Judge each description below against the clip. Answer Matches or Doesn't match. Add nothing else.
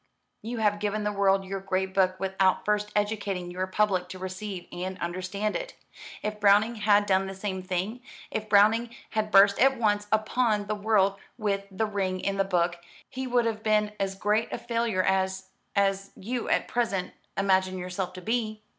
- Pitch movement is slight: Matches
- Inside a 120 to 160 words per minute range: Doesn't match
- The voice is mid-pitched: Doesn't match